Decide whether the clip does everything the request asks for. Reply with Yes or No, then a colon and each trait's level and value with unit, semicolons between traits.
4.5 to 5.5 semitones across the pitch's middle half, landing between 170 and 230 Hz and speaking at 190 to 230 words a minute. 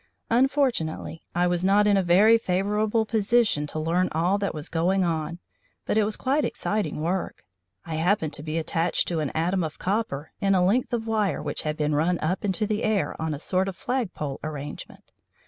Yes: average, 4.8 semitones; medium, 185 Hz; average, 200 wpm